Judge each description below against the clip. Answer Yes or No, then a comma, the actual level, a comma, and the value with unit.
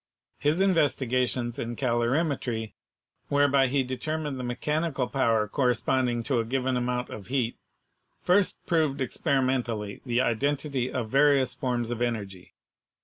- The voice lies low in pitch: Yes, low, 130 Hz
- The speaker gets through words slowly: Yes, slow, 130 wpm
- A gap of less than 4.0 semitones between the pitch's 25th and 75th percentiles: Yes, average, 2.9 semitones